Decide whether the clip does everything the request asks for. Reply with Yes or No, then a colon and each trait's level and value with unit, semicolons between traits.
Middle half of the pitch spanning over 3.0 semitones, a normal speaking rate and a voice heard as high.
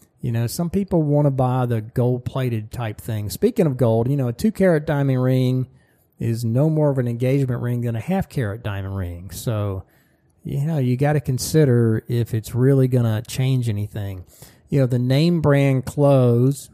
No: average, 3.5 semitones; average, 195 wpm; low, 125 Hz